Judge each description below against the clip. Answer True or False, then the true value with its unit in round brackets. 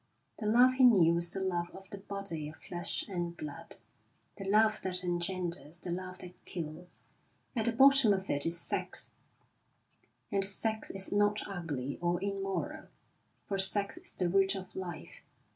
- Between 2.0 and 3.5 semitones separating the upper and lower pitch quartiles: True (2.6 semitones)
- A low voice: False (190 Hz)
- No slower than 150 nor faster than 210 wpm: True (165 wpm)